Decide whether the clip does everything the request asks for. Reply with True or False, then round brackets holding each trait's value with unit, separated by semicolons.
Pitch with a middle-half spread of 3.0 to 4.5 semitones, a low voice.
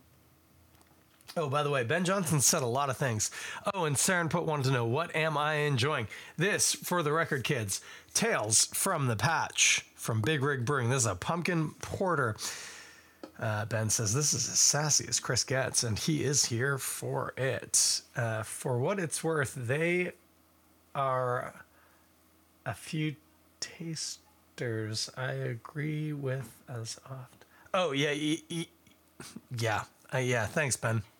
False (5.5 semitones; 130 Hz)